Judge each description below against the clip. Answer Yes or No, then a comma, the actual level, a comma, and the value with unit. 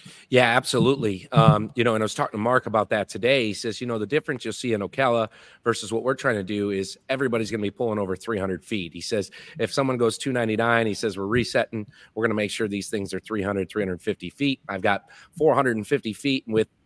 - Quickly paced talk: Yes, fast, 230 wpm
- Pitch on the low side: Yes, low, 110 Hz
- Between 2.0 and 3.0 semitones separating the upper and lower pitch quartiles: No, average, 3.4 semitones